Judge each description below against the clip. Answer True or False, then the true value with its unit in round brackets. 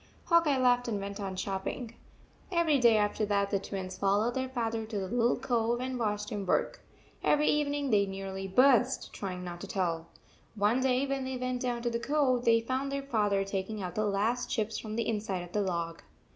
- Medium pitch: False (220 Hz)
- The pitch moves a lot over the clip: False (4.3 semitones)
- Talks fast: True (215 wpm)